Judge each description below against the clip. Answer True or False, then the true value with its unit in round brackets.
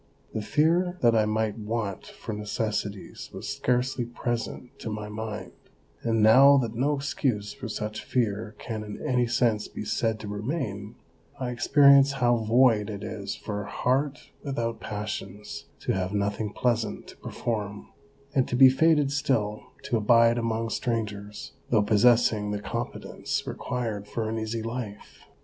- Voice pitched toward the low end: True (115 Hz)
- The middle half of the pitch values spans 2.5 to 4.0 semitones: True (2.9 semitones)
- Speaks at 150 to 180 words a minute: True (155 wpm)